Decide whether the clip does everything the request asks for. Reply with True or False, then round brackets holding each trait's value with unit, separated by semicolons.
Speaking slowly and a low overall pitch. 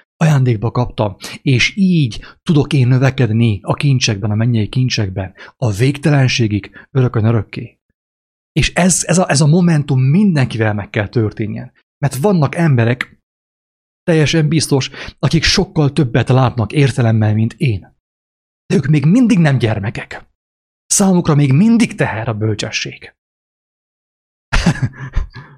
True (120 wpm; 130 Hz)